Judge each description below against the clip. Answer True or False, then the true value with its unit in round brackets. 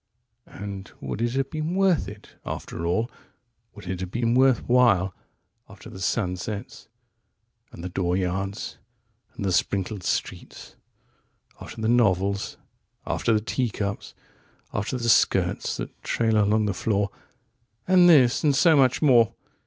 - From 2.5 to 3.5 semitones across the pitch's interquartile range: False (4.3 semitones)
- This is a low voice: True (110 Hz)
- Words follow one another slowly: True (130 wpm)